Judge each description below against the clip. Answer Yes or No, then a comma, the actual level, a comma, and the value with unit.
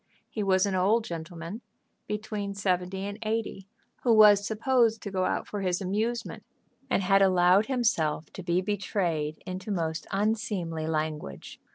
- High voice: Yes, high, 195 Hz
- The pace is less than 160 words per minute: Yes, average, 150 wpm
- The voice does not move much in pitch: No, average, 3.3 semitones